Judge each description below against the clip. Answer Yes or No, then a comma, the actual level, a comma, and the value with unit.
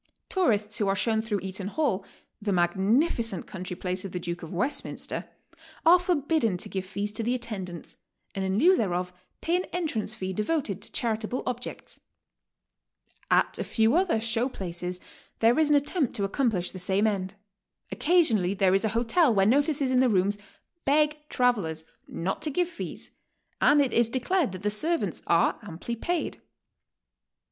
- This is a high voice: Yes, high, 220 Hz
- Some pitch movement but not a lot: No, wide, 6.8 semitones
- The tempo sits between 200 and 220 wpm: No, average, 170 wpm